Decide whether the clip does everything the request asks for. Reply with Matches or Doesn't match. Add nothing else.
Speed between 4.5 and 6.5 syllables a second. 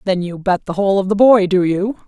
Matches